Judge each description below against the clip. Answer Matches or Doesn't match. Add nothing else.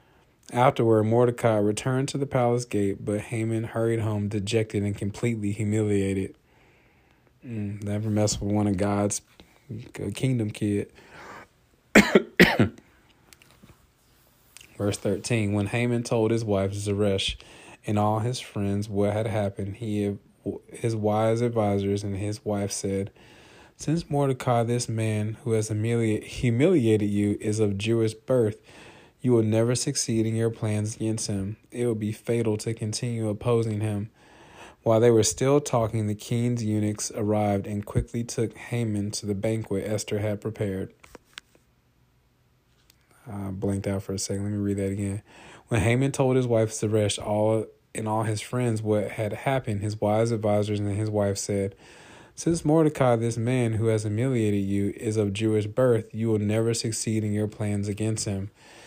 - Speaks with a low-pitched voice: Matches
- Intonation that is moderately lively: Doesn't match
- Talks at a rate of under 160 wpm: Matches